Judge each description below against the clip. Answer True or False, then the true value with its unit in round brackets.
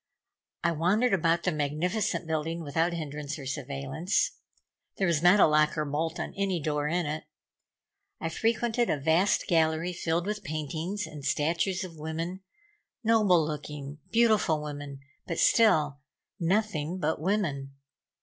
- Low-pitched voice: False (165 Hz)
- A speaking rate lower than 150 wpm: True (140 wpm)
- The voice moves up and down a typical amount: True (3.6 semitones)